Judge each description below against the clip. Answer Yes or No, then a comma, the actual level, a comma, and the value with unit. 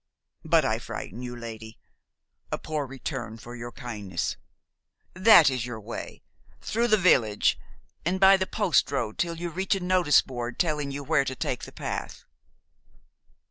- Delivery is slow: No, average, 155 wpm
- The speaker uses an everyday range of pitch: No, wide, 6.9 semitones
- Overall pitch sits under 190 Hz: Yes, low, 135 Hz